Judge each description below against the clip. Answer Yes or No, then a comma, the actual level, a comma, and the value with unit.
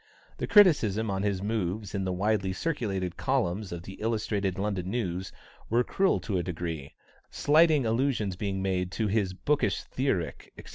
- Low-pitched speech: Yes, low, 100 Hz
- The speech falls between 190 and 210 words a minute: No, average, 160 wpm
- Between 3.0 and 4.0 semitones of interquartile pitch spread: Yes, average, 3.7 semitones